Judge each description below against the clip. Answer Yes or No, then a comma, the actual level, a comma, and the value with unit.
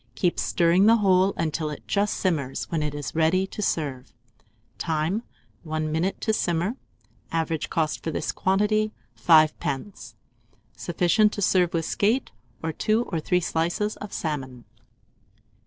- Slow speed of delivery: No, average, 145 wpm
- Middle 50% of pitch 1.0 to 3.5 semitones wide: No, average, 4.1 semitones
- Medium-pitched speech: Yes, medium, 170 Hz